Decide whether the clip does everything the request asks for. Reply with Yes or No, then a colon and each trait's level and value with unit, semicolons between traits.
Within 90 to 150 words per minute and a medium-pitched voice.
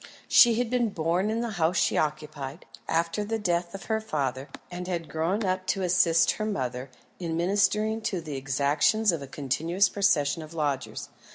No: average, 180 wpm; medium, 170 Hz